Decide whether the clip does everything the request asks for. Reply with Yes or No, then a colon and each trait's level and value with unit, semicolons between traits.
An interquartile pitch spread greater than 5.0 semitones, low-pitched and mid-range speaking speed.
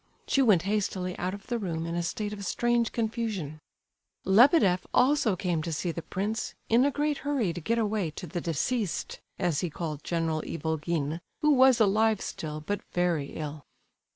No: wide, 5.5 semitones; high, 190 Hz; average, 180 wpm